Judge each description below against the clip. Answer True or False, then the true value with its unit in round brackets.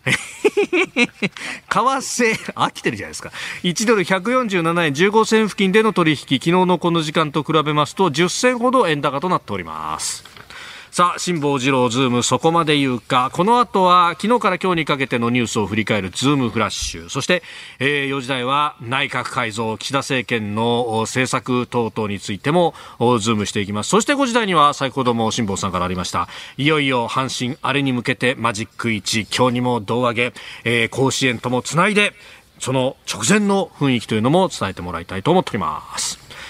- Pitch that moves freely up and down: True (7.1 semitones)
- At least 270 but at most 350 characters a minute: False (360 characters per minute)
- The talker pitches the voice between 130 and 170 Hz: True (135 Hz)